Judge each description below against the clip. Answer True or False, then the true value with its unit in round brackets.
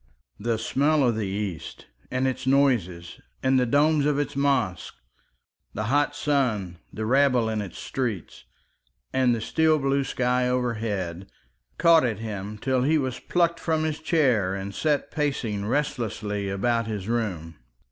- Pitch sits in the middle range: False (125 Hz)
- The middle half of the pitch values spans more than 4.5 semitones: True (5.2 semitones)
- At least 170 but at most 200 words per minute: False (150 wpm)